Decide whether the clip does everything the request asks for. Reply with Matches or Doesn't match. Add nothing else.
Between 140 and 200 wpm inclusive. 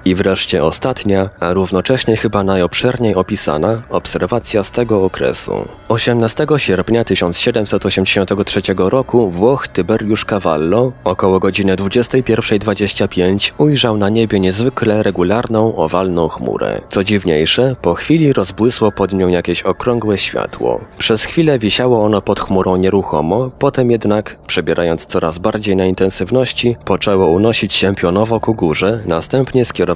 Doesn't match